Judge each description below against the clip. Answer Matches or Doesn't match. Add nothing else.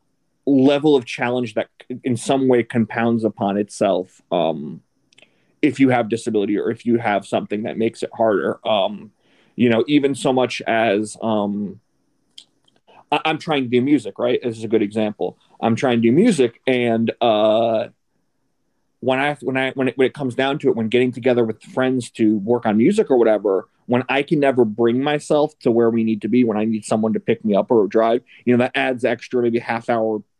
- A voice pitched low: Matches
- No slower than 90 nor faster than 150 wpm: Doesn't match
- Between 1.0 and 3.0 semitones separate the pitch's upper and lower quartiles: Matches